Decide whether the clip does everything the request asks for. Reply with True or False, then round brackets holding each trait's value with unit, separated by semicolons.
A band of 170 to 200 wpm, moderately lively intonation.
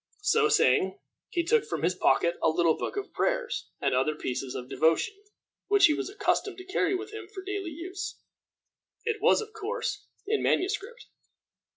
False (175 wpm; 8.5 semitones)